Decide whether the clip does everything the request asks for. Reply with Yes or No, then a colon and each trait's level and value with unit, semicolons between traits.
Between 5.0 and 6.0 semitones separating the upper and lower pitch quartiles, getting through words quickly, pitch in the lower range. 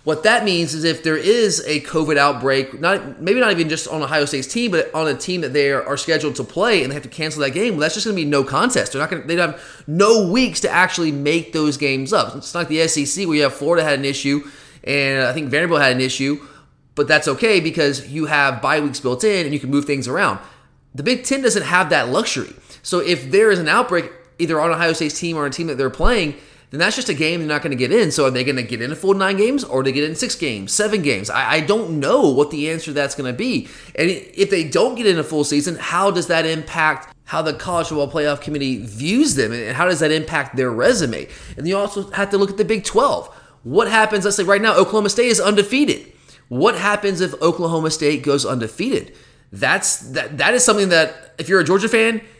No: wide, 5.4 semitones; fast, 255 wpm; medium, 155 Hz